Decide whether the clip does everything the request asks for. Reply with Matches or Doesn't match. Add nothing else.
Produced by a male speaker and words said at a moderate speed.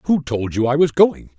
Doesn't match